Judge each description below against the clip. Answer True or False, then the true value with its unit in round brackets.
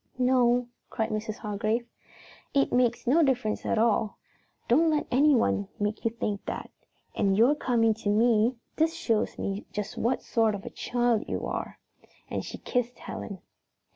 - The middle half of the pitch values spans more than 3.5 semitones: False (2.8 semitones)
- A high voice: True (230 Hz)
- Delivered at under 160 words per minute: False (165 wpm)